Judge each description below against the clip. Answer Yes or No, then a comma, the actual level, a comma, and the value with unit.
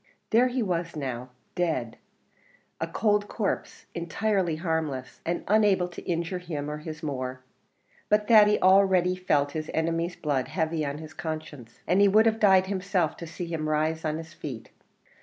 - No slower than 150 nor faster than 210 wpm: Yes, average, 165 wpm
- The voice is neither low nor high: Yes, medium, 165 Hz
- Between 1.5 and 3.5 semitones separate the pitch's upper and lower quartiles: No, average, 3.9 semitones